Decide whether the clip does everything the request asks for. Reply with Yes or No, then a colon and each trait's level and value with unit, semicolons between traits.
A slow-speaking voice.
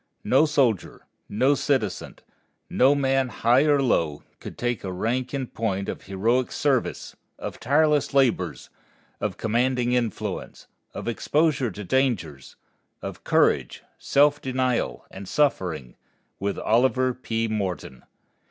Yes: slow, 120 wpm